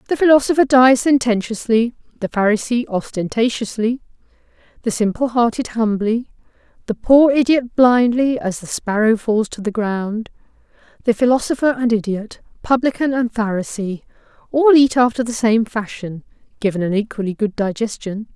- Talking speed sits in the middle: No, slow, 120 wpm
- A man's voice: No, female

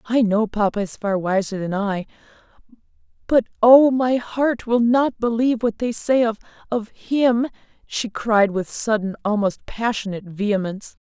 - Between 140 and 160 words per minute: Yes, average, 145 wpm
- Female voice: Yes, female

